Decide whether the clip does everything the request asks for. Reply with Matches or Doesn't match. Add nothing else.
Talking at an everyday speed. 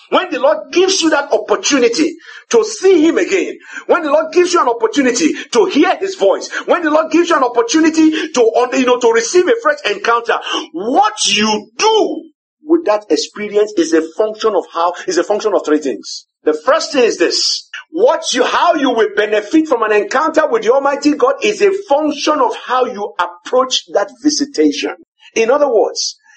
Matches